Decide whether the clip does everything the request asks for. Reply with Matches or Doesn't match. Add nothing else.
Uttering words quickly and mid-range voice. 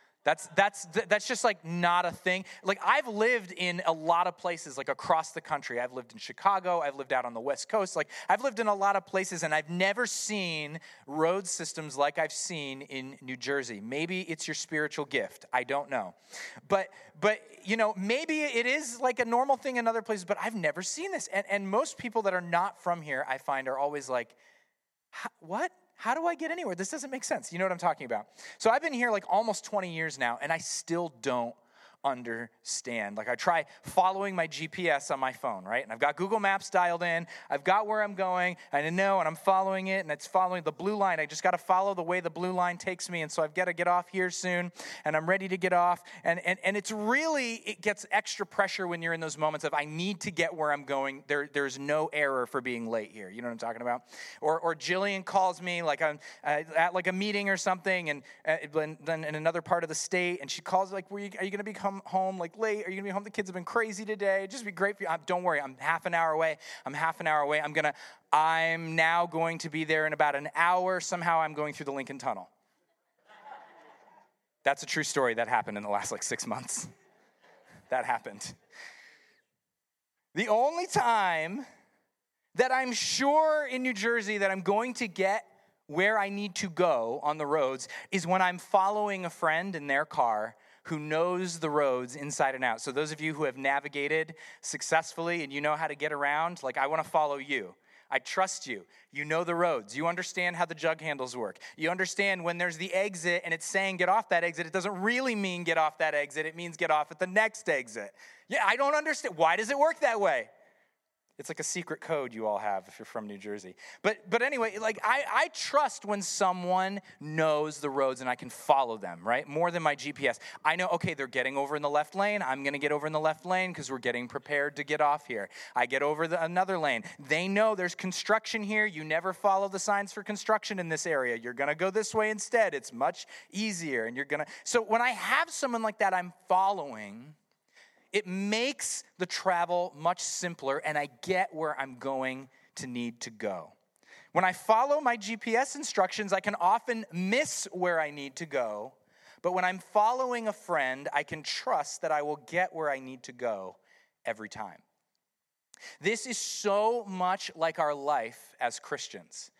Matches